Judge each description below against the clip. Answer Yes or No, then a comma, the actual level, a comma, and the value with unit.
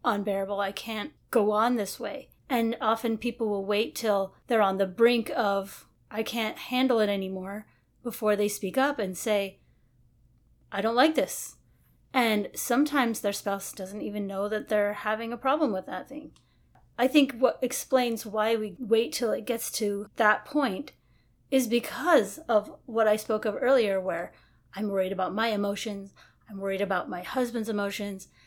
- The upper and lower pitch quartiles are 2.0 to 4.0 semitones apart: Yes, average, 3.0 semitones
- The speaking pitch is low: No, high, 215 Hz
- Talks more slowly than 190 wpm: Yes, average, 170 wpm